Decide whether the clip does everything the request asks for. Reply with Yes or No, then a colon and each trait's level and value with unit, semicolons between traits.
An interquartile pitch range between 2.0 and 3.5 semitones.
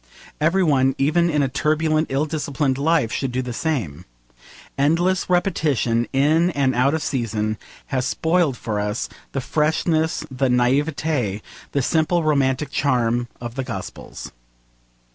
No: average, 4.2 semitones